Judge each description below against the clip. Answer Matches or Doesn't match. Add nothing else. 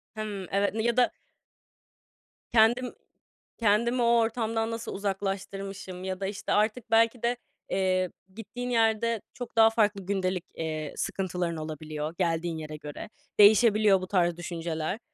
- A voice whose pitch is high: Matches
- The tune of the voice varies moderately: Matches